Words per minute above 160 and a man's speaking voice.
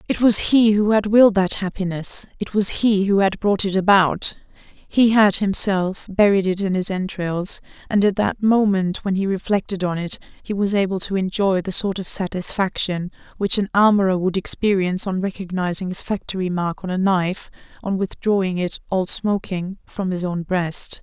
No: average, 185 wpm; female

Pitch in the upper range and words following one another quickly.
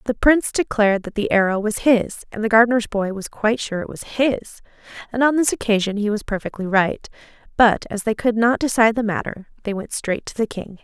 Yes: high, 220 Hz; fast, 215 wpm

